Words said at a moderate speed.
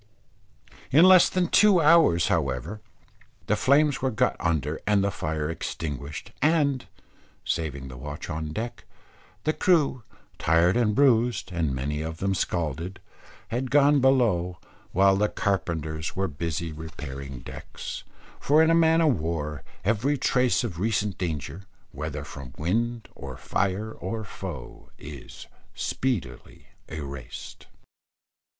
No: slow, 130 wpm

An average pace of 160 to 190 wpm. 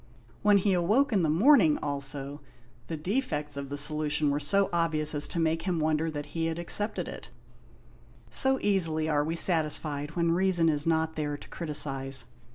Yes: average, 175 wpm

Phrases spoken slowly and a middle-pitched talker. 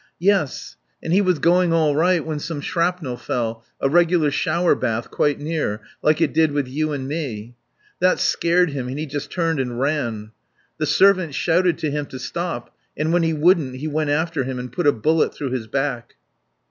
No: average, 200 wpm; medium, 150 Hz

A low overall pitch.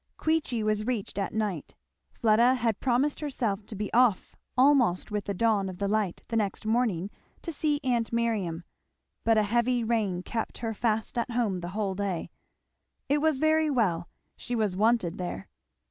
No: high, 220 Hz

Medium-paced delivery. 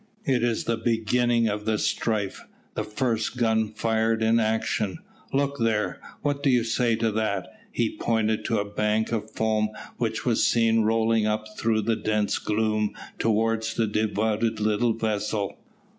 Yes: average, 160 wpm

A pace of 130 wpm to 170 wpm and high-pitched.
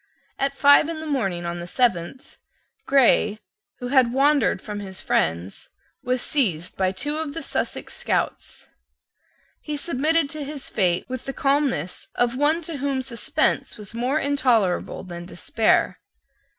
Yes: average, 150 wpm; very high, 255 Hz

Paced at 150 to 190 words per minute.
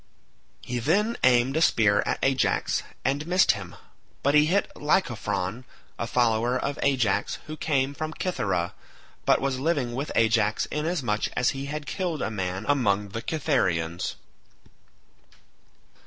No: average, 140 wpm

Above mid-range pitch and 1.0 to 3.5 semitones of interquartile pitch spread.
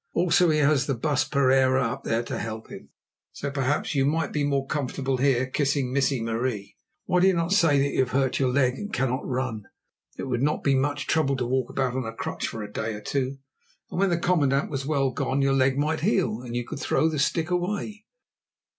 No: low, 135 Hz; average, 2.9 semitones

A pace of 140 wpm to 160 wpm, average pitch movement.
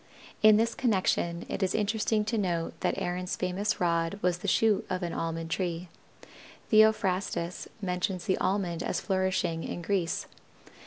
Yes: average, 150 wpm; average, 3.0 semitones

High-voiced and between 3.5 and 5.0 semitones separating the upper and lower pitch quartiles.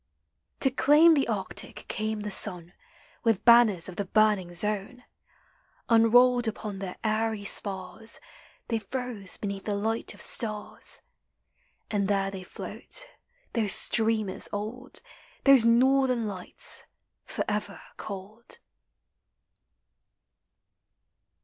No: high, 215 Hz; average, 3.1 semitones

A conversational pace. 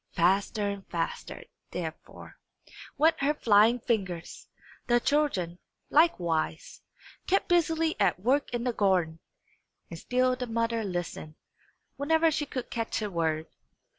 No: slow, 125 wpm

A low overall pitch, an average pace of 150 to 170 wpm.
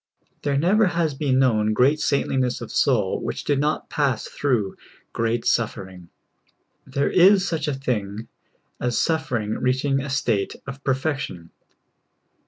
No: low, 130 Hz; slow, 135 wpm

